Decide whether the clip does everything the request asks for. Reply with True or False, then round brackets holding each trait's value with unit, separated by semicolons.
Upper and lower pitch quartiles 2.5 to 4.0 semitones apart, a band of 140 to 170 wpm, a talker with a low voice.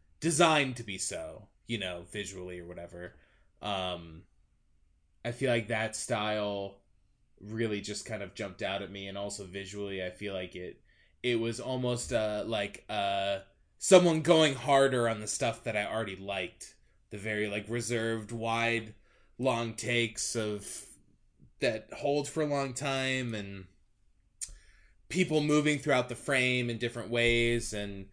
True (3.7 semitones; 150 wpm; 110 Hz)